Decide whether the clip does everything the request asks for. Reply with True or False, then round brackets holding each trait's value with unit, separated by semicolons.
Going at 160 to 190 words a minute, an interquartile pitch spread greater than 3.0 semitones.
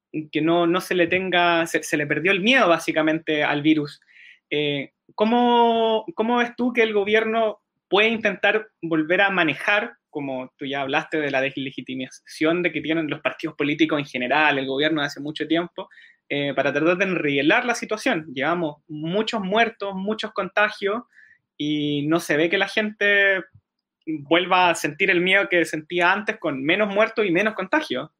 True (175 wpm; 5.5 semitones)